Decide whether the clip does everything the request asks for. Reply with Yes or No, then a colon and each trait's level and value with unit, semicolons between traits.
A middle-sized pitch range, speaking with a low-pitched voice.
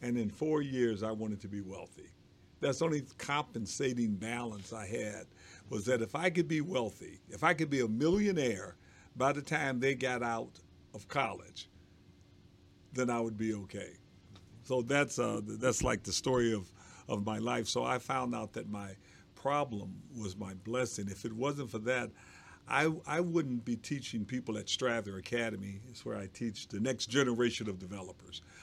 Yes: average, 4.4 semitones; low, 115 Hz